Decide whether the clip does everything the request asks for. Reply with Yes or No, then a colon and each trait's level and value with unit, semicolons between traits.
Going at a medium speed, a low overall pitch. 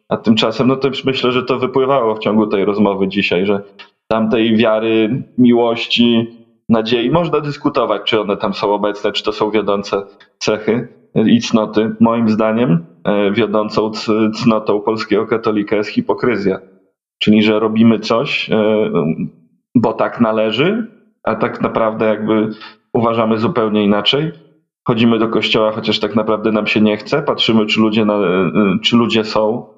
Yes: average, 145 wpm; low, 110 Hz